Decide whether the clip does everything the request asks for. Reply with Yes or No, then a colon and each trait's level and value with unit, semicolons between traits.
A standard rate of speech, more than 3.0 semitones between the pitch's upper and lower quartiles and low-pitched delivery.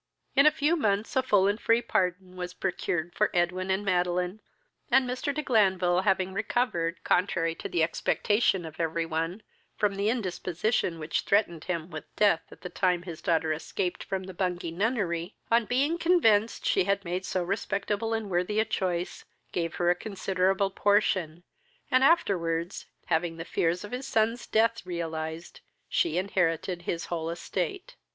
No: average, 165 wpm; average, 3.7 semitones; medium, 185 Hz